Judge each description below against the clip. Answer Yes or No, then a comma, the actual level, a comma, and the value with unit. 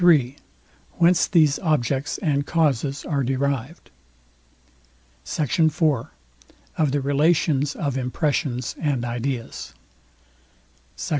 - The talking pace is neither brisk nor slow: No, slow, 95 wpm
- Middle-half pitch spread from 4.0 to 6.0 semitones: No, average, 2.9 semitones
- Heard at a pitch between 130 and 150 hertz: Yes, medium, 140 Hz